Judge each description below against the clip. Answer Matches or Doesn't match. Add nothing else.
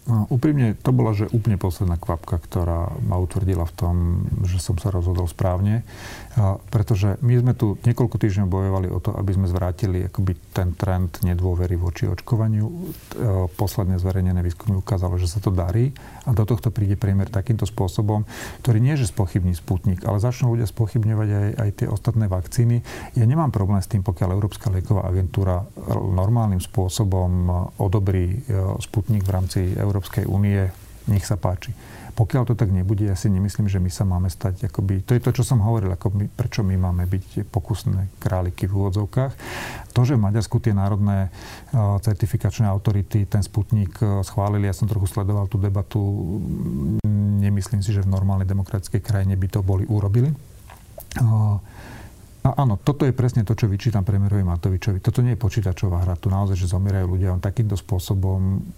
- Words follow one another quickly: Matches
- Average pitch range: Matches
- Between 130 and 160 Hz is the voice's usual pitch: Doesn't match